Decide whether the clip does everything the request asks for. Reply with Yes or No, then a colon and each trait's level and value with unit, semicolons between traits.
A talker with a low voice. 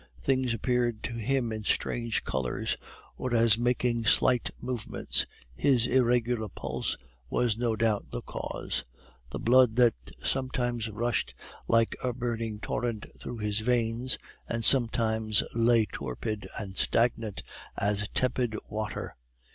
Yes: low, 115 Hz